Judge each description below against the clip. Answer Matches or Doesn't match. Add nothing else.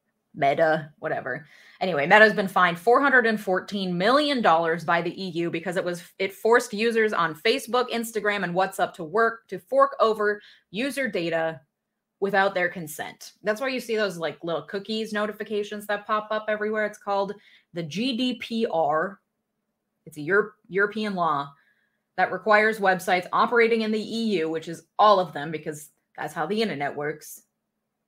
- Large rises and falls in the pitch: Doesn't match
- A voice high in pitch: Matches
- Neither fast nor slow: Matches